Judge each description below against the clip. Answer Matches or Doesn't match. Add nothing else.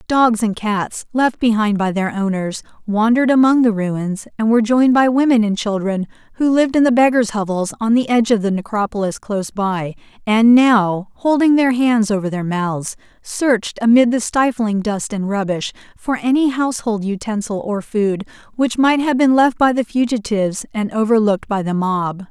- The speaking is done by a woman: Matches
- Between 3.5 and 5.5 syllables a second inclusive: Matches